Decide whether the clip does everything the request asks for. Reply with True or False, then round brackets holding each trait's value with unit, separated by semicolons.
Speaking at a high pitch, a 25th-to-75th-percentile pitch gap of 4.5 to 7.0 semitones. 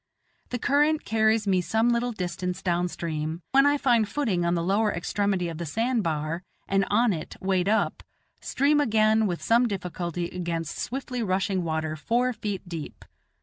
True (195 Hz; 5.1 semitones)